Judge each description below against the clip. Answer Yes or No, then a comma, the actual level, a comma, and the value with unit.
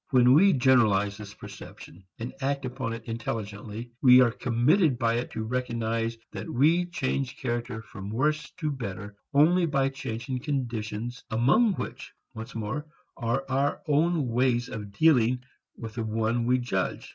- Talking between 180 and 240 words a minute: No, average, 155 wpm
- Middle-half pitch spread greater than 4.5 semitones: No, average, 3.3 semitones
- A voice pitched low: Yes, low, 120 Hz